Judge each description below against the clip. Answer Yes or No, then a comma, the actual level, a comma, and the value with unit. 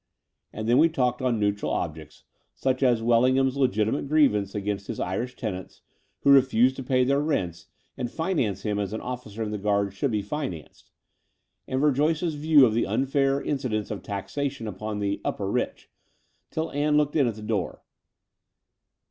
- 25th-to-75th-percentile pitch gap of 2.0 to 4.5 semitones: No, average, 5.0 semitones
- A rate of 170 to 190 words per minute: Yes, average, 175 wpm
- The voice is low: Yes, low, 120 Hz